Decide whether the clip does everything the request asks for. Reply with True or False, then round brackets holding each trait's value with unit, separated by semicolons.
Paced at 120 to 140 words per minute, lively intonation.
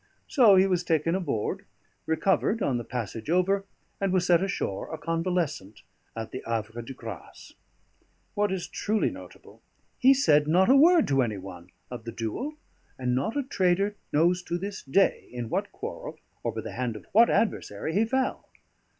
False (175 wpm; 8.5 semitones)